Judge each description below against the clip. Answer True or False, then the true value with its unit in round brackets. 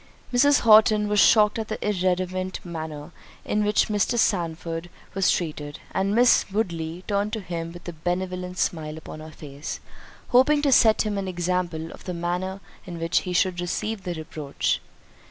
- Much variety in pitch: False (4.0 semitones)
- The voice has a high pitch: False (180 Hz)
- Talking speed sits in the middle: True (165 wpm)